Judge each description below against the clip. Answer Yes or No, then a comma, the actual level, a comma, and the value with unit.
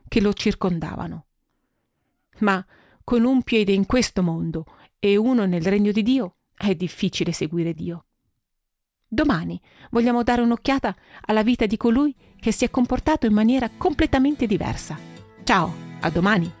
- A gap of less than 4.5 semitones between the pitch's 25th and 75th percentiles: No, wide, 5.4 semitones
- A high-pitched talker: Yes, high, 215 Hz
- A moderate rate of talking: Yes, average, 140 wpm